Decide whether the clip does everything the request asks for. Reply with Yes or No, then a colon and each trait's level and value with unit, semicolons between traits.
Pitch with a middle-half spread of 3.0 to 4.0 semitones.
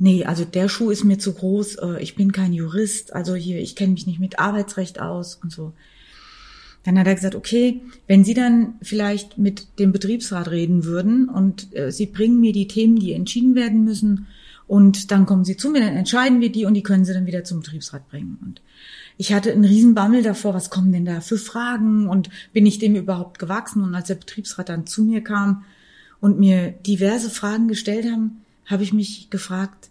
No: narrow, 2.6 semitones